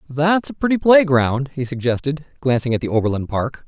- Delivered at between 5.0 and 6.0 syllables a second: Yes, 5.4 syllables/s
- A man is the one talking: Yes, male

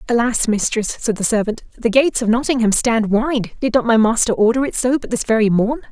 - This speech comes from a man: No, female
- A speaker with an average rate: No, fast, 225 wpm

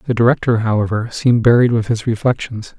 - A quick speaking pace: No, average, 170 wpm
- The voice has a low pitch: Yes, low, 115 Hz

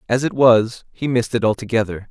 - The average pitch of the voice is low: Yes, low, 115 Hz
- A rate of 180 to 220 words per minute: Yes, average, 200 wpm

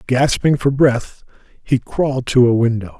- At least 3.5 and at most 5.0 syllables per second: Yes, 4.5 syllables/s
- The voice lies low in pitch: Yes, low, 125 Hz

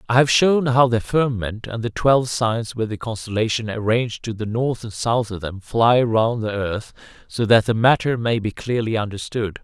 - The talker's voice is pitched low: Yes, low, 115 Hz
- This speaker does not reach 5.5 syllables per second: Yes, 5.0 syllables/s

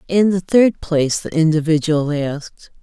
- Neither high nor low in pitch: Yes, medium, 165 Hz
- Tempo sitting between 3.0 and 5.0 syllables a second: Yes, 4.7 syllables/s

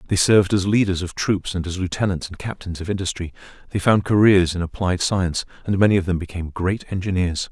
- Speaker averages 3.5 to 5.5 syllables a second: No, 6.1 syllables/s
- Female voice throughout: No, male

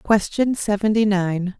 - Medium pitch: No, high, 205 Hz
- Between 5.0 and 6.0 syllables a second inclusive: No, 3.9 syllables/s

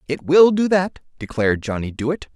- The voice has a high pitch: No, medium, 150 Hz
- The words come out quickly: No, average, 180 wpm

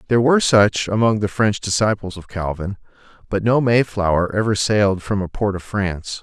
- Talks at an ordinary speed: Yes, average, 185 wpm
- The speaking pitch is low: Yes, low, 100 Hz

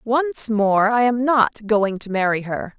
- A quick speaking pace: No, average, 195 wpm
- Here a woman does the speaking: Yes, female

